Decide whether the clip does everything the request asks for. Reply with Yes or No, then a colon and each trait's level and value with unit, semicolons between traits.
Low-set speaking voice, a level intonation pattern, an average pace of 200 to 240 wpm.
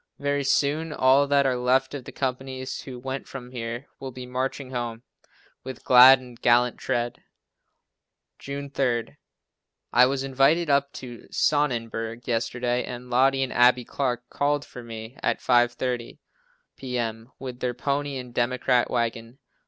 No: low, 125 Hz; narrow, 1.9 semitones; average, 145 wpm